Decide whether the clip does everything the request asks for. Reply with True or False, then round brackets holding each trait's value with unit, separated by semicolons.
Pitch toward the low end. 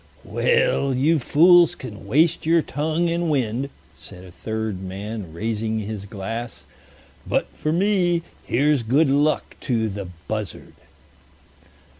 True (130 Hz)